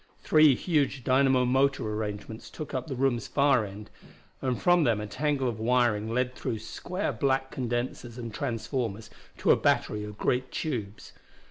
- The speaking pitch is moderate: No, low, 125 Hz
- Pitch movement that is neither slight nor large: Yes, average, 3.6 semitones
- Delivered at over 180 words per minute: No, average, 160 wpm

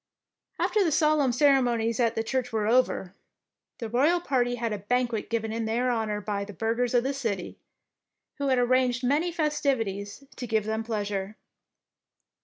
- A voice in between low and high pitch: No, high, 240 Hz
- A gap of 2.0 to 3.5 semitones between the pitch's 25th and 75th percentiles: Yes, average, 3.1 semitones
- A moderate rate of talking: Yes, average, 165 wpm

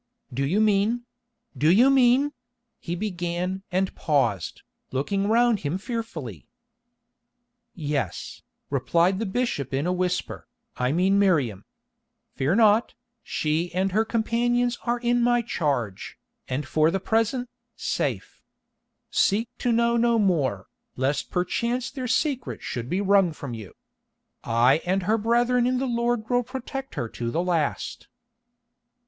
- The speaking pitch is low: No, high, 195 Hz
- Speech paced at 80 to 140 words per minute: Yes, slow, 135 wpm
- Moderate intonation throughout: No, wide, 7.5 semitones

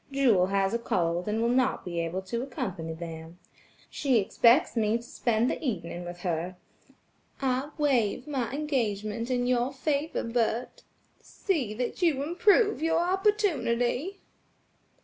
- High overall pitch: Yes, high, 240 Hz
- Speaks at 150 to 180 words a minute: No, average, 140 wpm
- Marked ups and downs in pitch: Yes, wide, 6.1 semitones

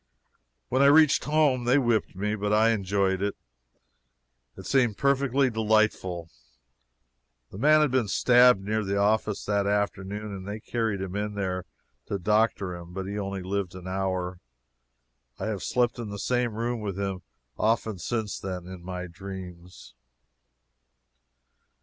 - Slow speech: No, average, 150 wpm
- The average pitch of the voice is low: Yes, low, 105 Hz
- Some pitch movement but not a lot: Yes, average, 3.5 semitones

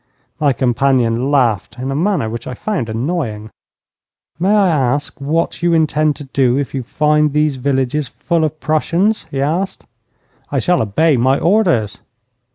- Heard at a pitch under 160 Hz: Yes, medium, 140 Hz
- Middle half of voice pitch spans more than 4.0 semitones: Yes, average, 4.5 semitones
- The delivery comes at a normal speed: Yes, average, 160 wpm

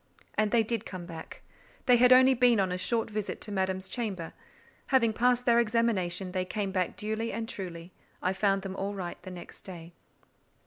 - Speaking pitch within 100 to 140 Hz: No, high, 200 Hz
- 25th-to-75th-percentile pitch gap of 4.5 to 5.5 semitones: No, average, 3.9 semitones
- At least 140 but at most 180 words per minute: No, average, 190 wpm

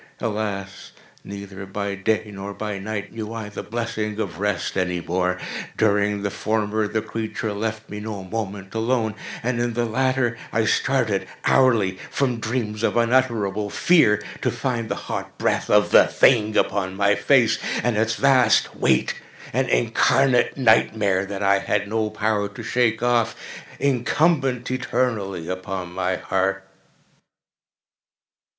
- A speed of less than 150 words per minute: Yes, average, 140 wpm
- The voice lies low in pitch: Yes, low, 110 Hz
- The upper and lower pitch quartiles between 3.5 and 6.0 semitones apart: No, average, 2.9 semitones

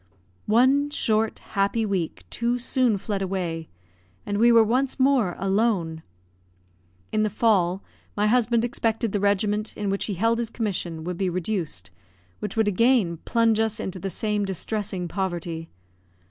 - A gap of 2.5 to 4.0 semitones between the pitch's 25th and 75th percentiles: Yes, average, 3.6 semitones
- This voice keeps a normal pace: Yes, average, 150 wpm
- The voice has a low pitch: No, high, 210 Hz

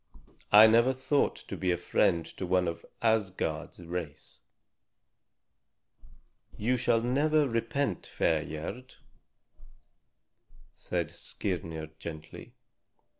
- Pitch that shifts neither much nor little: No, wide, 6.3 semitones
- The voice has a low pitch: Yes, very low, 95 Hz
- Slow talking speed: Yes, slow, 95 wpm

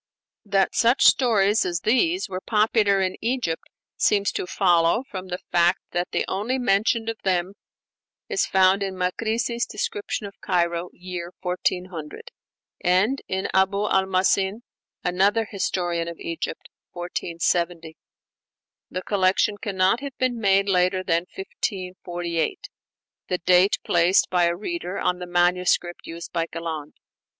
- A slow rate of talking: Yes, slow, 130 wpm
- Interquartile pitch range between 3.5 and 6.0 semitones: No, average, 3.1 semitones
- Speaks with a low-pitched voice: No, high, 190 Hz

